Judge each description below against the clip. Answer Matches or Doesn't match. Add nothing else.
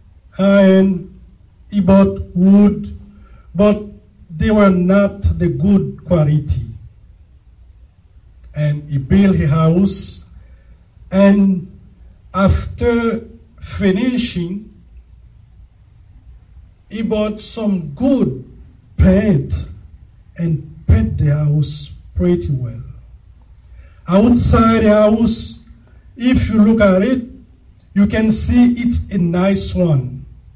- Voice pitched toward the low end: Doesn't match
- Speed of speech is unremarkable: Doesn't match